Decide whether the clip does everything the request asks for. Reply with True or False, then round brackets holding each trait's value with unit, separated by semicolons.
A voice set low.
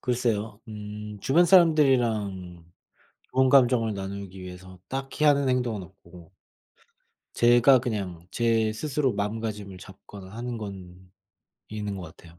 True (105 Hz)